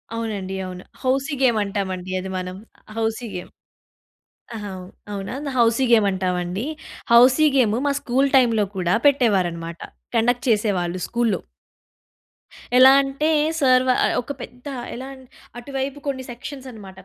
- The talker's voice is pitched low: No, high, 230 Hz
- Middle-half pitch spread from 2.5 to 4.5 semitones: No, average, 5.2 semitones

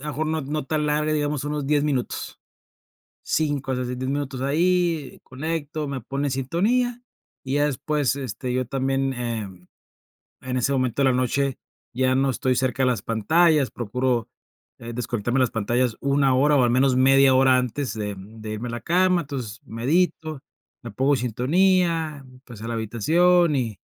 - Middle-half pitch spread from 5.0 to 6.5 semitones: No, average, 3.4 semitones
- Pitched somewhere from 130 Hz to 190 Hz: Yes, low, 135 Hz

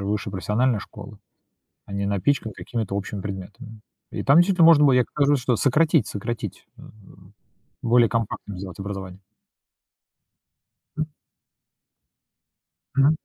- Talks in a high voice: No, low, 115 Hz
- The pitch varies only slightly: No, average, 5.3 semitones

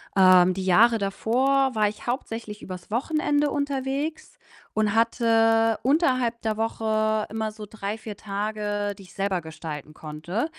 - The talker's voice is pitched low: No, high, 220 Hz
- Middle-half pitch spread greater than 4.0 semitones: No, average, 3.3 semitones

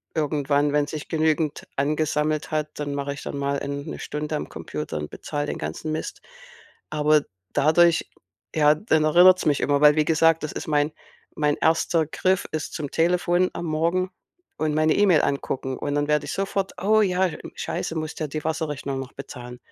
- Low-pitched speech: No, medium, 155 Hz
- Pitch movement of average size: No, narrow, 1.9 semitones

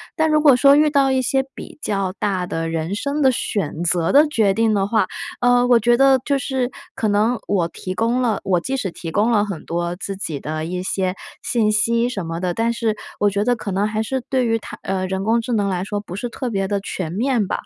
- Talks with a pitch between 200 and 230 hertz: Yes, high, 215 Hz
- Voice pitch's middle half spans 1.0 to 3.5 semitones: No, average, 4.5 semitones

